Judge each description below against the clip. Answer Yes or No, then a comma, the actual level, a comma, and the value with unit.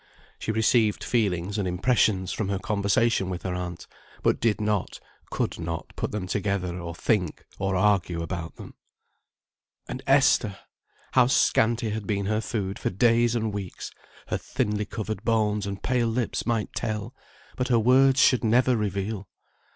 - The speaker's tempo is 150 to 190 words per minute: Yes, average, 160 wpm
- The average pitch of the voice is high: No, low, 105 Hz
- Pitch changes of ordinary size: Yes, average, 3.2 semitones